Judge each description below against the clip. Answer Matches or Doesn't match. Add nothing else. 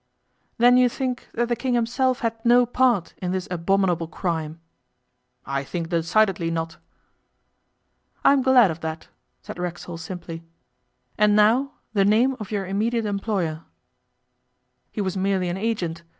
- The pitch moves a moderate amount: Doesn't match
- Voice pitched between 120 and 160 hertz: Doesn't match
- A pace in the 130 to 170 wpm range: Matches